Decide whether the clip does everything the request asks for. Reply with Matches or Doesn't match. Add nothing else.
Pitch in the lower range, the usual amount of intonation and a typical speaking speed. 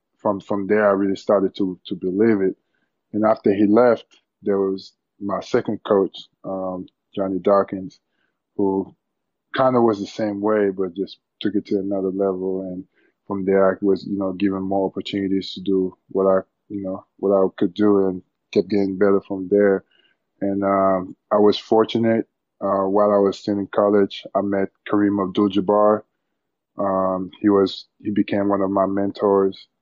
Doesn't match